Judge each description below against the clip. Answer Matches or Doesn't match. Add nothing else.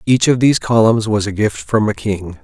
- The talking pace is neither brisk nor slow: Doesn't match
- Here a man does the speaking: Matches